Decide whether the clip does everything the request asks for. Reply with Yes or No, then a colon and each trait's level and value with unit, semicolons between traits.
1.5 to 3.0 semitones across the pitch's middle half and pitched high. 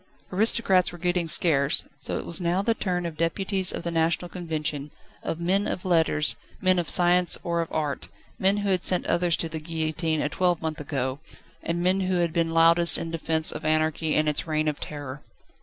No: narrow, 2.4 semitones; medium, 165 Hz